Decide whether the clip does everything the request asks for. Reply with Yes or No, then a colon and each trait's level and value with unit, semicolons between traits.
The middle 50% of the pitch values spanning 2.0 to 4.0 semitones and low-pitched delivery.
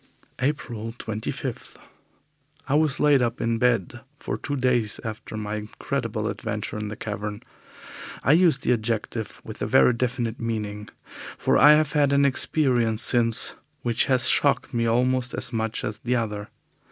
Yes: average, 3.0 semitones; low, 115 Hz